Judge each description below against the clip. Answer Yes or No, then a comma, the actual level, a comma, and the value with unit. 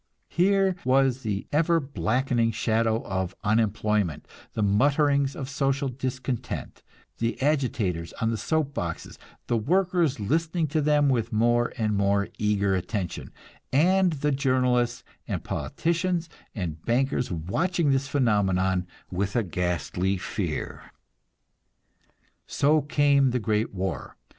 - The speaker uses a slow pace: Yes, slow, 120 wpm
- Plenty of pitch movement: Yes, wide, 5.8 semitones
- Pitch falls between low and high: No, low, 125 Hz